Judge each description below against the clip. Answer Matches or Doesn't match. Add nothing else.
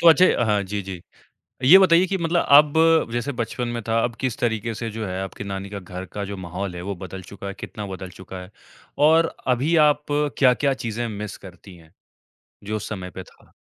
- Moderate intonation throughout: Doesn't match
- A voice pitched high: Doesn't match